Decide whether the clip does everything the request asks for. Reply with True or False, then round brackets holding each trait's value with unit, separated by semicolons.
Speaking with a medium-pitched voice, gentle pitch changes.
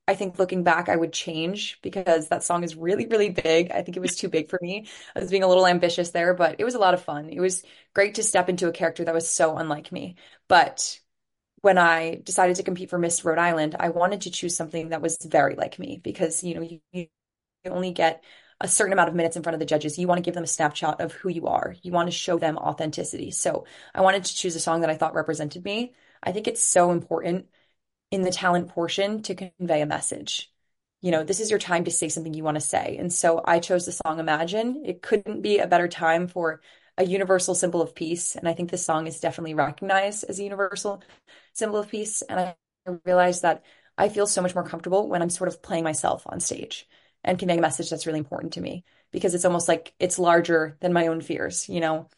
True (175 Hz; 2.2 semitones)